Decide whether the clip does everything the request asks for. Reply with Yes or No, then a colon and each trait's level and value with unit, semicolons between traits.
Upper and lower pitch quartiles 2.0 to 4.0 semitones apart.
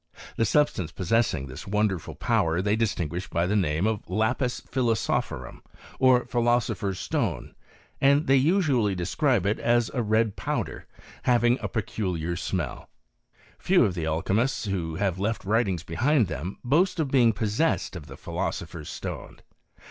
No: average, 5.1 semitones